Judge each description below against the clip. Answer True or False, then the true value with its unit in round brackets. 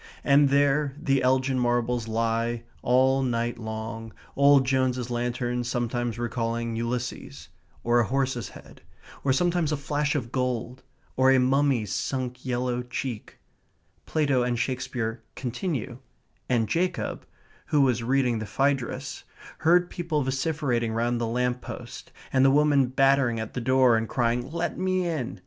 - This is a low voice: True (125 Hz)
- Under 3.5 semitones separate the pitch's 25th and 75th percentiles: True (2.5 semitones)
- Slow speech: False (145 wpm)